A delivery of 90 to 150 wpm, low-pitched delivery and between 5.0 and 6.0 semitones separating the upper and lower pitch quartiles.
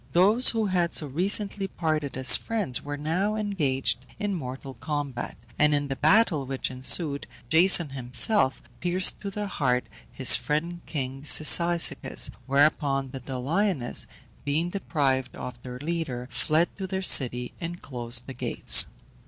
No: average, 145 wpm; medium, 150 Hz; wide, 5.4 semitones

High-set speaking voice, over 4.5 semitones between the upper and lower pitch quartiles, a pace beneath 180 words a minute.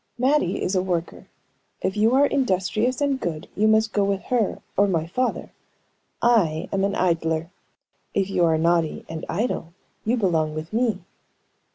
Yes: high, 195 Hz; average, 5.3 semitones; average, 165 wpm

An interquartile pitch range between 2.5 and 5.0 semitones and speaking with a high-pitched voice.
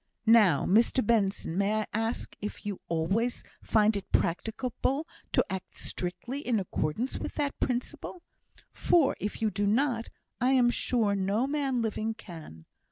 Yes: average, 3.9 semitones; high, 220 Hz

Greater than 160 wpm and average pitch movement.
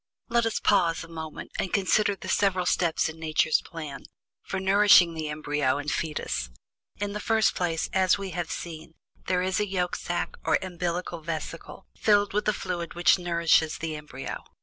Yes: average, 175 wpm; average, 3.2 semitones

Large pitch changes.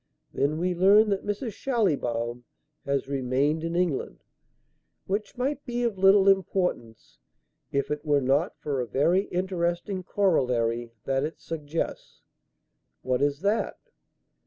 Yes: wide, 6.2 semitones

